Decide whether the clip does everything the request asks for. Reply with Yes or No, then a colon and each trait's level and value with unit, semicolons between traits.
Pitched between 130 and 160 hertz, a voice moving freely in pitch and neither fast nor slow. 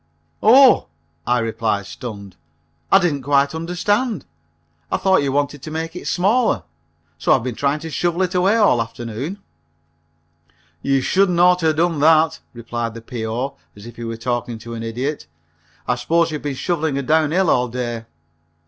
Yes: medium, 140 Hz; wide, 6.4 semitones; average, 170 wpm